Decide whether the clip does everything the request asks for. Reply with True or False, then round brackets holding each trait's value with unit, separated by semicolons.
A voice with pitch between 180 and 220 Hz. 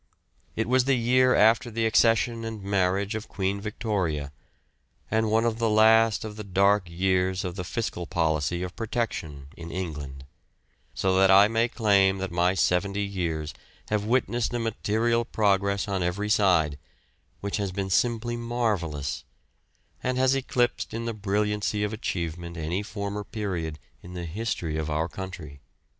False (100 Hz)